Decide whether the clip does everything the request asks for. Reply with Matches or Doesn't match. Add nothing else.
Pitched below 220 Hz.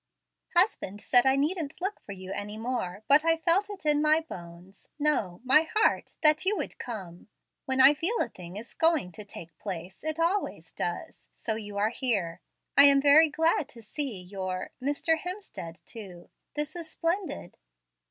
Doesn't match